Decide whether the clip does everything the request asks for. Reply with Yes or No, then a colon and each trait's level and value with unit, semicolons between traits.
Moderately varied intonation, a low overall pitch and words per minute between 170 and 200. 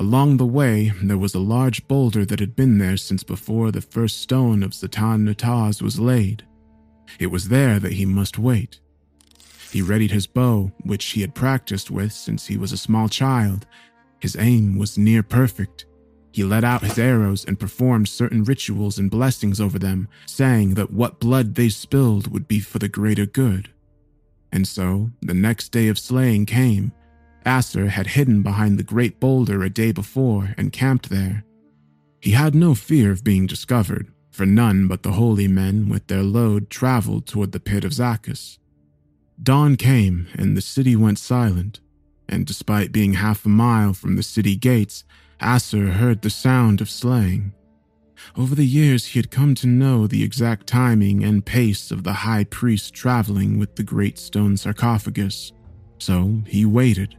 Yes: average, 3.5 semitones; low, 105 Hz; average, 175 wpm